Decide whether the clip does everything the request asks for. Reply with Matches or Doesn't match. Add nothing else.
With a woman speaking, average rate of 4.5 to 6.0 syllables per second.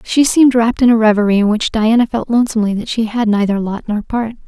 Doesn't match